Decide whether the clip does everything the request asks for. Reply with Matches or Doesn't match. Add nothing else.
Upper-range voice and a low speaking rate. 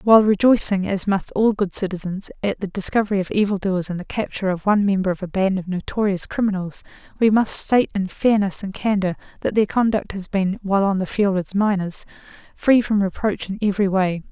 Doesn't match